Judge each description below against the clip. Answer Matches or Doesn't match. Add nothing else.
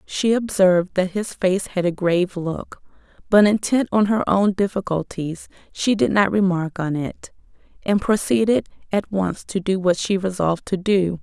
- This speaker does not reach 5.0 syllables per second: Matches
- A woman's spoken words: Matches